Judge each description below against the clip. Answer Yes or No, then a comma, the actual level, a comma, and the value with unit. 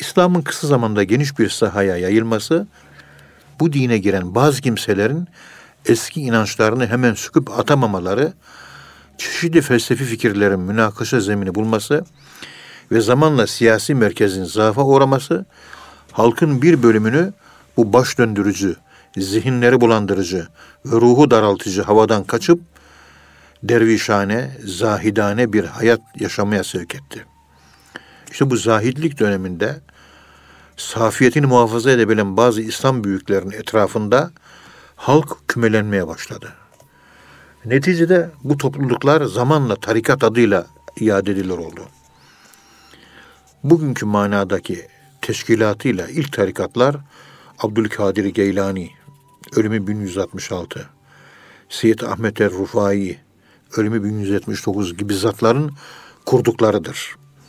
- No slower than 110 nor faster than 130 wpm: No, slow, 95 wpm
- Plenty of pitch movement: No, average, 4.8 semitones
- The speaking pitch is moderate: No, low, 115 Hz